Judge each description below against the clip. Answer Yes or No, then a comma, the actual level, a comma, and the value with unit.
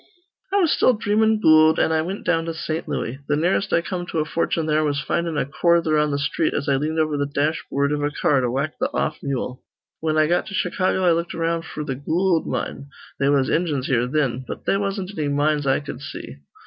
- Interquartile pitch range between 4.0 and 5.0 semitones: No, average, 3.1 semitones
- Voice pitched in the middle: Yes, medium, 155 Hz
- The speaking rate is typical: No, fast, 240 wpm